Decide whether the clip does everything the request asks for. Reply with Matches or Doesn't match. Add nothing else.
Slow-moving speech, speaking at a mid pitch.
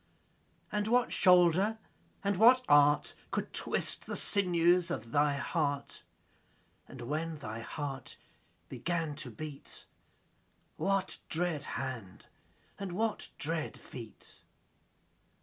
Matches